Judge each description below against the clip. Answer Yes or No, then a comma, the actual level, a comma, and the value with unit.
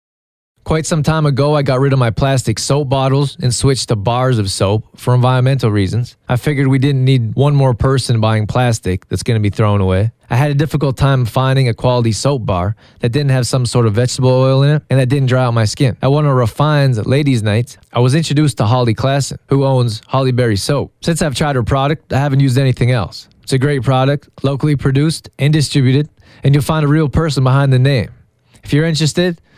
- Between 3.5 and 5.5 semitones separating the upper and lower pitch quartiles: No, average, 2.7 semitones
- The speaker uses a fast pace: Yes, fast, 225 wpm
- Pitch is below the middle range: Yes, low, 130 Hz